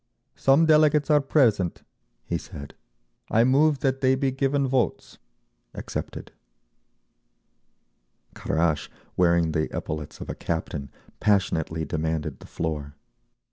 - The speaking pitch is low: Yes, low, 100 Hz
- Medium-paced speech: No, slow, 110 wpm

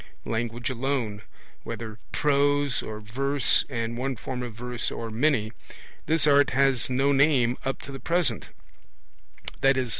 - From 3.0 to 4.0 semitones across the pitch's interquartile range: Yes, average, 3.3 semitones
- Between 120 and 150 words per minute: Yes, average, 140 wpm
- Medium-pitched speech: No, low, 130 Hz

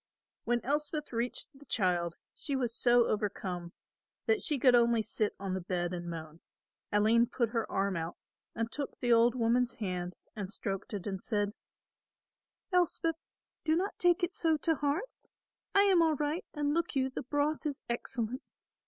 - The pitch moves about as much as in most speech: No, wide, 6.7 semitones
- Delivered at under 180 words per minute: Yes, average, 170 wpm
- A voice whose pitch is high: Yes, high, 240 Hz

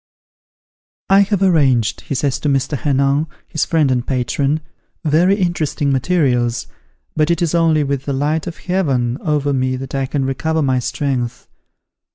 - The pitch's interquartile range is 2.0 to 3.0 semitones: No, average, 3.4 semitones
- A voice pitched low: No, medium, 145 Hz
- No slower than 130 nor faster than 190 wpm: Yes, average, 160 wpm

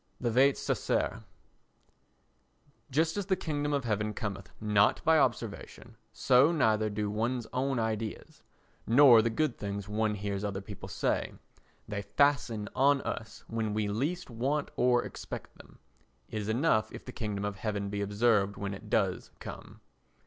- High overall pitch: No, low, 110 Hz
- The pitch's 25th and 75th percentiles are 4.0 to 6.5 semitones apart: Yes, average, 4.3 semitones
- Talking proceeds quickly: No, average, 155 wpm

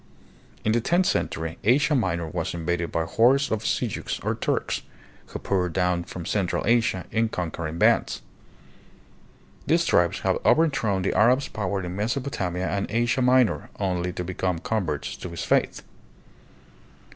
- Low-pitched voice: Yes, very low, 95 Hz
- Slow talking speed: No, average, 150 wpm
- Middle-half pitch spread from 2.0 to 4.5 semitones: No, average, 5.1 semitones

